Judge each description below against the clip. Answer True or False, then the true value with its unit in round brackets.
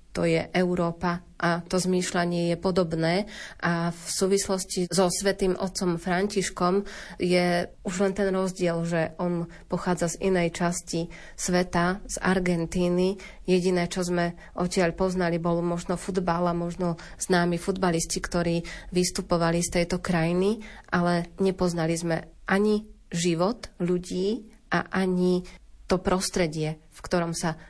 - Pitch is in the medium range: True (180 Hz)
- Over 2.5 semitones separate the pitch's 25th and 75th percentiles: False (1.7 semitones)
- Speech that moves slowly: False (130 wpm)